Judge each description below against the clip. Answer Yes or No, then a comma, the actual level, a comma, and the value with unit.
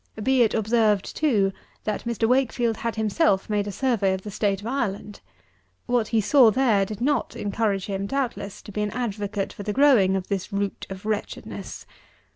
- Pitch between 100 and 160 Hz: No, high, 210 Hz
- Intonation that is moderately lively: Yes, average, 3.2 semitones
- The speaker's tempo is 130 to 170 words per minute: No, average, 185 wpm